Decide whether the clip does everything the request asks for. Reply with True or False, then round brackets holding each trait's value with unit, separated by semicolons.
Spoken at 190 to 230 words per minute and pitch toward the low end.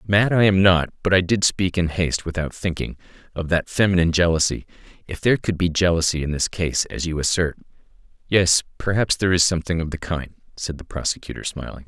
True (195 wpm; 85 Hz)